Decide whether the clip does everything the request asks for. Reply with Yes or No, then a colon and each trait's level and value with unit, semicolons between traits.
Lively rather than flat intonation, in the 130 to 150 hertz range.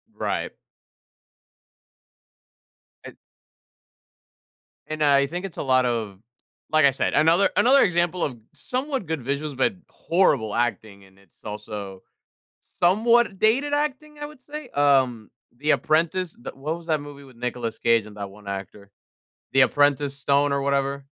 Yes: wide, 6.8 semitones; medium, 140 Hz